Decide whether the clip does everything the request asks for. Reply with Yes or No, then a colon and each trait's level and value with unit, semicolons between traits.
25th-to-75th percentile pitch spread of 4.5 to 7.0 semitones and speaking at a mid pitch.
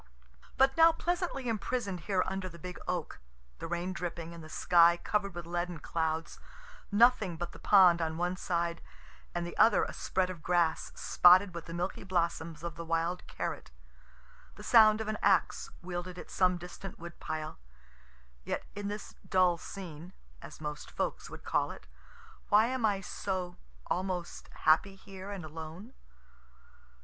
No: average, 2.7 semitones; medium, 180 Hz